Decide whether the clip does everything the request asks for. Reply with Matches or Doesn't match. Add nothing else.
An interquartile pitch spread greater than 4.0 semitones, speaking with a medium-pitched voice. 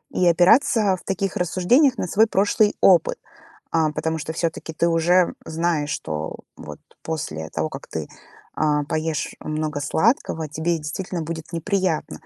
Doesn't match